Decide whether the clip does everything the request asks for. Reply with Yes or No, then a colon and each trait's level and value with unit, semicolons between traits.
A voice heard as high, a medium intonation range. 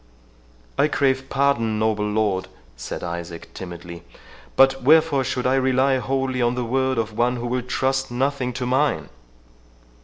No: low, 125 Hz; average, 3.4 semitones